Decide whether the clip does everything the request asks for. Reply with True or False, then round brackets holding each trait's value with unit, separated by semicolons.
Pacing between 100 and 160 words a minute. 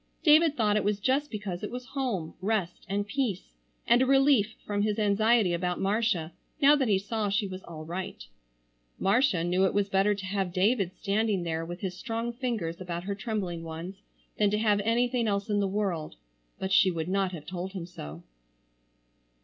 False (190 wpm)